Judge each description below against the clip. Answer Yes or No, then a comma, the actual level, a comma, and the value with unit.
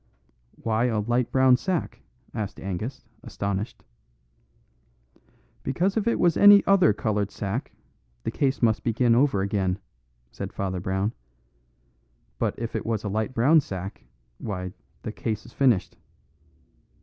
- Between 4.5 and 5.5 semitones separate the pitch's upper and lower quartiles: Yes, average, 4.8 semitones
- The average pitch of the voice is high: No, low, 110 Hz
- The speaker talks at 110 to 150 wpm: Yes, slow, 135 wpm